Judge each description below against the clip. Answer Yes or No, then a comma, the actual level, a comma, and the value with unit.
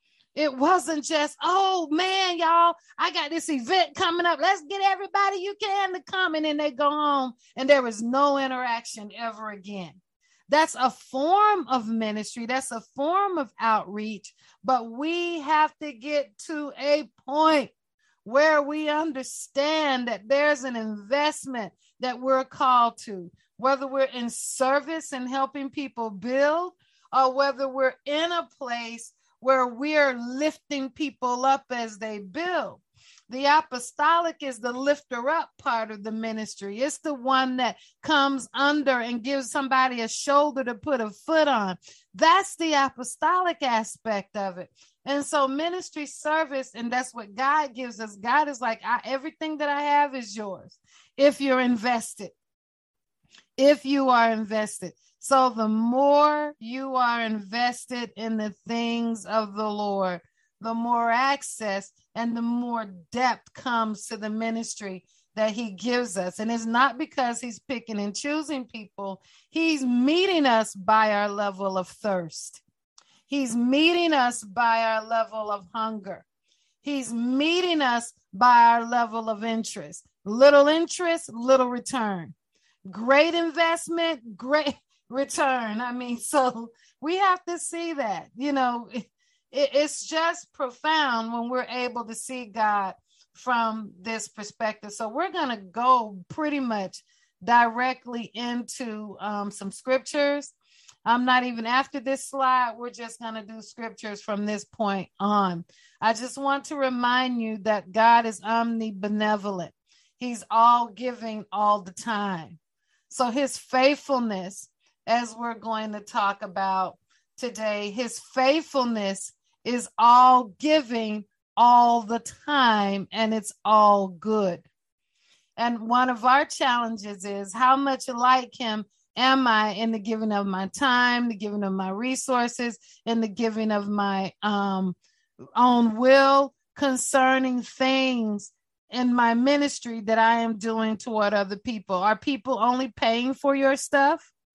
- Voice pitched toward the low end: No, high, 245 Hz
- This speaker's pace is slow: No, average, 145 wpm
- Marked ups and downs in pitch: No, average, 4.4 semitones